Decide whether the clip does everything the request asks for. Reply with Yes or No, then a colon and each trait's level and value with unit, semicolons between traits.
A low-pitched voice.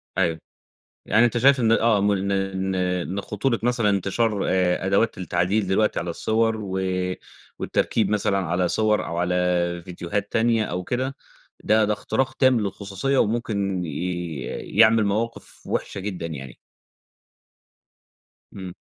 Yes: low, 100 Hz